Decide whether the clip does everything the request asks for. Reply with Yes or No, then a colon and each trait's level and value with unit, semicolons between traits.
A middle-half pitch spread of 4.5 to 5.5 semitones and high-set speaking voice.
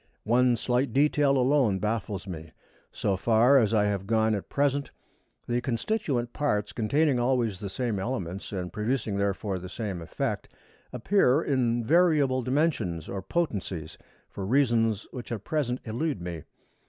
No: average, 5.0 semitones; low, 115 Hz